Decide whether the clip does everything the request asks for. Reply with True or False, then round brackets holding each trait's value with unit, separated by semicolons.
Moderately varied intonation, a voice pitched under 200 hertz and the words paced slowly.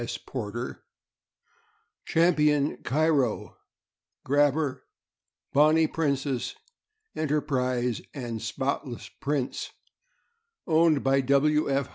True (3.1 semitones; 140 Hz; 75 wpm)